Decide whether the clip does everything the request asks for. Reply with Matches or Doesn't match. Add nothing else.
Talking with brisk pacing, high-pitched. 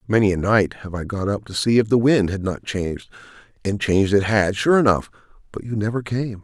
Doesn't match